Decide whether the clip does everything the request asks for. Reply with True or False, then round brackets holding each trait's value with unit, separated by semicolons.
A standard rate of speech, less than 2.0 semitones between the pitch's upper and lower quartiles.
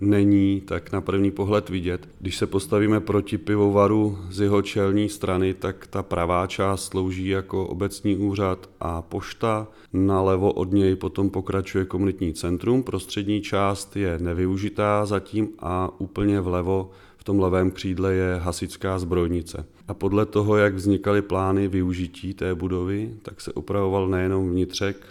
True (145 wpm; 1.5 semitones)